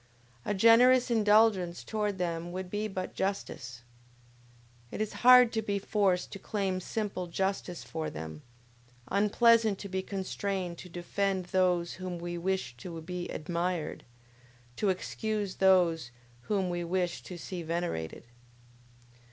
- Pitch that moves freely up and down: No, average, 2.9 semitones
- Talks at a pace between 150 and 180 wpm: No, slow, 135 wpm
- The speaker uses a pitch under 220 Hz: Yes, medium, 185 Hz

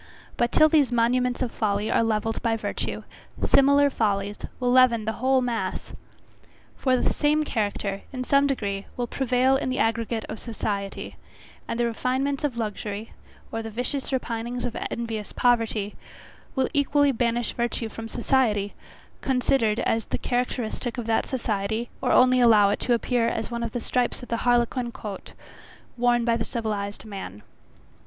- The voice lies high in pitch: Yes, high, 235 Hz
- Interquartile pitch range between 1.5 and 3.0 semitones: Yes, narrow, 2.4 semitones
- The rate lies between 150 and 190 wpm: Yes, average, 160 wpm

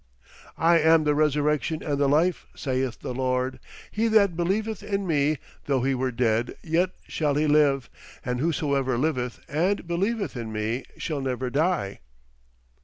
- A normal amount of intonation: Yes, average, 4.6 semitones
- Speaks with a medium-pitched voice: Yes, medium, 145 Hz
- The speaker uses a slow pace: No, average, 155 wpm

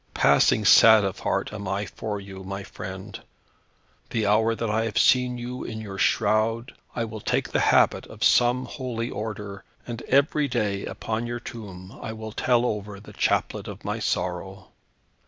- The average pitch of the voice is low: Yes, low, 110 Hz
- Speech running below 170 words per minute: No, average, 175 wpm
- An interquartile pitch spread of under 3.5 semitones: Yes, average, 3.0 semitones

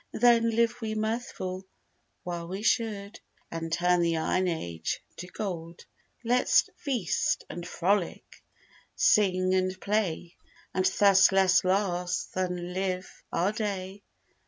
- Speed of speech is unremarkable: No, slow, 120 wpm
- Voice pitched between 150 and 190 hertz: Yes, medium, 185 Hz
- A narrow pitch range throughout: No, average, 3.0 semitones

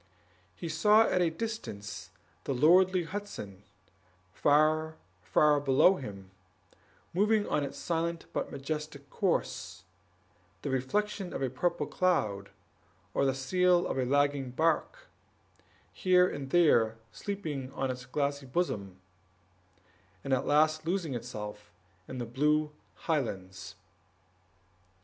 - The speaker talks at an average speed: No, slow, 120 wpm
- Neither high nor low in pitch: Yes, medium, 145 Hz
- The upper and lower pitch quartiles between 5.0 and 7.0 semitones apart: Yes, wide, 5.4 semitones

